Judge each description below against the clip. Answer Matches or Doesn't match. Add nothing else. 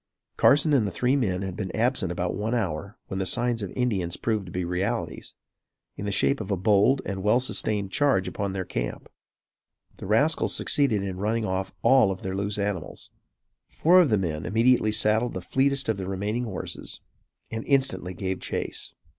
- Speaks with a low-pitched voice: Matches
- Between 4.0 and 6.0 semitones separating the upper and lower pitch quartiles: Matches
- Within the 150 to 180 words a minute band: Doesn't match